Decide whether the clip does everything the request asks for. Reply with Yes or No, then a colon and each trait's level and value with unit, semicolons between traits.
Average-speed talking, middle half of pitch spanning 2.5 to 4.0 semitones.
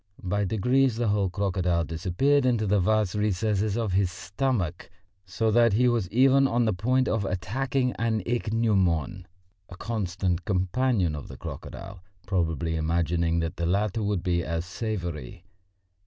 No: average, 150 wpm; average, 4.4 semitones